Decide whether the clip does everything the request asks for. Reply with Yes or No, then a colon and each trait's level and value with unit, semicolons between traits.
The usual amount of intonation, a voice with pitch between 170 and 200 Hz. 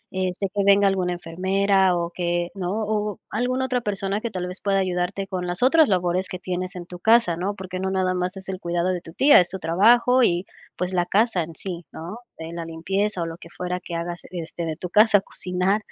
No: narrow, 2.3 semitones; medium, 185 Hz